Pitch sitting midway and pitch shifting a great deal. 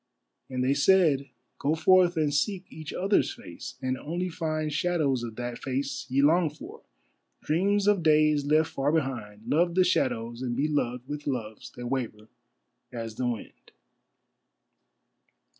No: medium, 145 Hz; average, 4.5 semitones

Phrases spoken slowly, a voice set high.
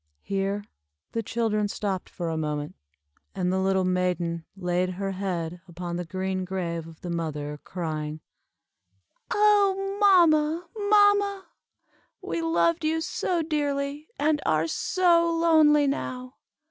Yes: slow, 125 wpm; high, 200 Hz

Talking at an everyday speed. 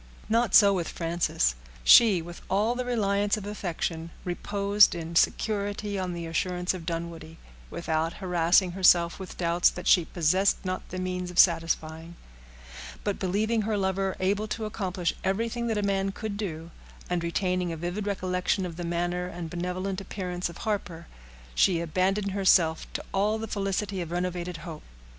Yes: average, 160 wpm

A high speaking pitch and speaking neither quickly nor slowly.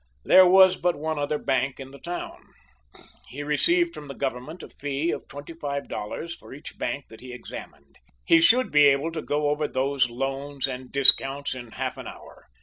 No: medium, 145 Hz; average, 195 wpm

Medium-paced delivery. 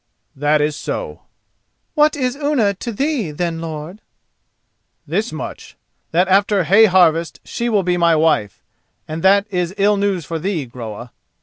Yes: average, 150 wpm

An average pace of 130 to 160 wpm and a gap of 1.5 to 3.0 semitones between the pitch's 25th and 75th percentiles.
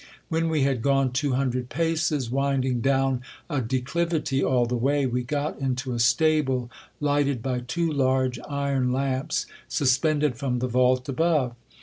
Yes: average, 150 wpm; narrow, 2.4 semitones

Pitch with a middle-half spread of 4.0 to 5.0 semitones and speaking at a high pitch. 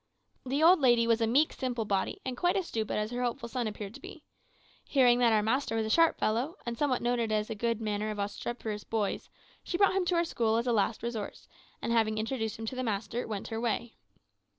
No: average, 2.7 semitones; high, 230 Hz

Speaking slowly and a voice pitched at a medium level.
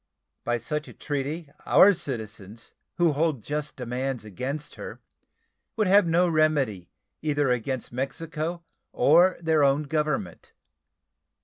Yes: slow, 120 wpm; medium, 145 Hz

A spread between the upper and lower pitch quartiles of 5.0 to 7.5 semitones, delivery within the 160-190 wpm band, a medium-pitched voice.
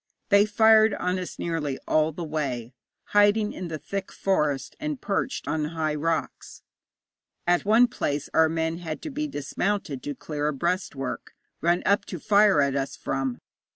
Yes: wide, 5.5 semitones; average, 165 wpm; medium, 165 Hz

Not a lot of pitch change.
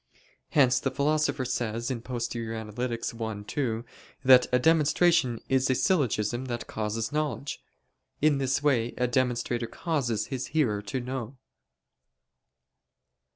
No: average, 3.2 semitones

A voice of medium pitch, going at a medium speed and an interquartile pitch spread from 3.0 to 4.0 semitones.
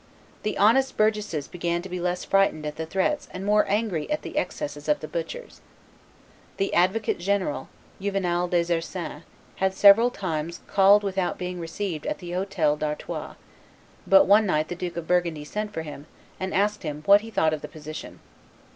Yes: medium, 180 Hz; average, 180 wpm; average, 3.7 semitones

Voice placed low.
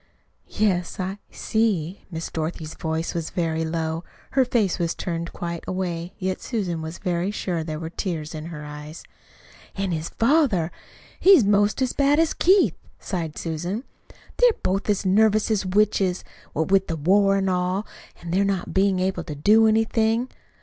No: medium, 185 Hz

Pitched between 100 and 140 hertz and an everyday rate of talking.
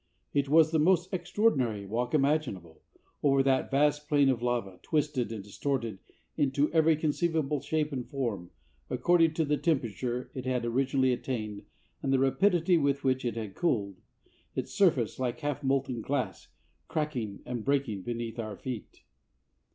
Yes: low, 135 Hz; average, 150 wpm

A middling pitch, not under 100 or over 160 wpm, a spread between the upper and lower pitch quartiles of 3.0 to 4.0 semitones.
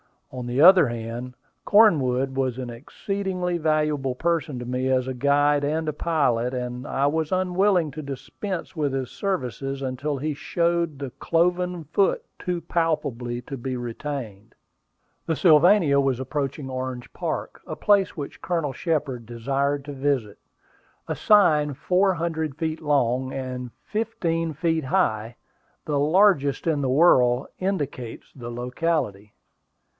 No: medium, 145 Hz; slow, 135 wpm; average, 4.6 semitones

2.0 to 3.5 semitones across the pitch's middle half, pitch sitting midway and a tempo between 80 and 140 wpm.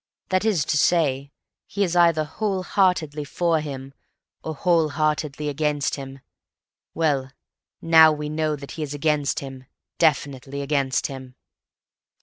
Yes: average, 2.7 semitones; medium, 150 Hz; slow, 135 wpm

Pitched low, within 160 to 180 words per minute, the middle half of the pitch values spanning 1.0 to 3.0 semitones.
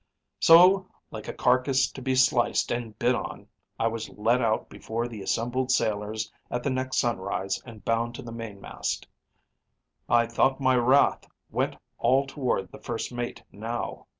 Yes: low, 120 Hz; average, 165 wpm; narrow, 2.6 semitones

